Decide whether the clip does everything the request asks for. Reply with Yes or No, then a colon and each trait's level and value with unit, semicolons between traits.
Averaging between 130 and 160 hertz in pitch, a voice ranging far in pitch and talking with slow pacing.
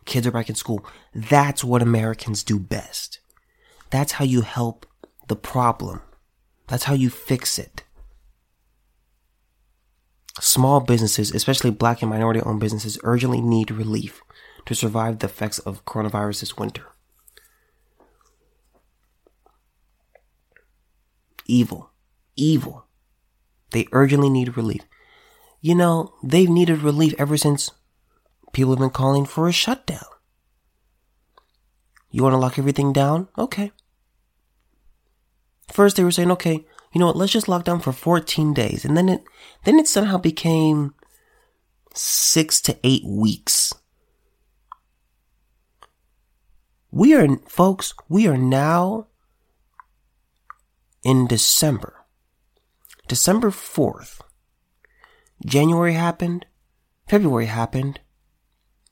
Yes: low, 135 Hz; wide, 7.1 semitones; slow, 110 wpm